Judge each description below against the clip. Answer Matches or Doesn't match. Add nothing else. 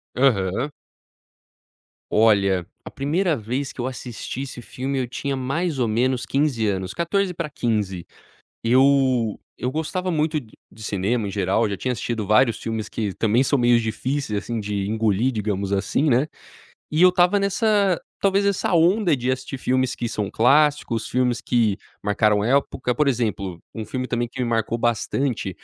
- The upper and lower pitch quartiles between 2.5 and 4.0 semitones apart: Doesn't match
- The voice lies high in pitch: Doesn't match